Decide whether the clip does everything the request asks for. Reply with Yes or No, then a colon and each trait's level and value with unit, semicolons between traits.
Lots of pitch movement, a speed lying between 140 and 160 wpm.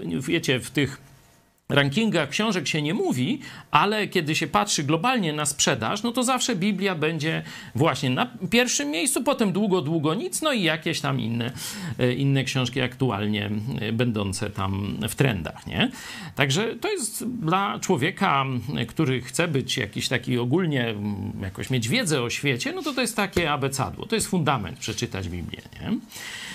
Yes: wide, 7.6 semitones; average, 155 wpm